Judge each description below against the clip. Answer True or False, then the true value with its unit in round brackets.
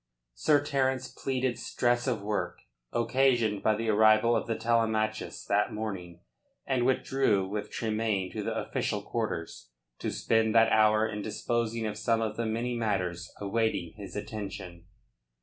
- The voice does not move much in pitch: True (2.3 semitones)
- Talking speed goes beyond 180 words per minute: False (150 wpm)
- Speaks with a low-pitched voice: True (110 Hz)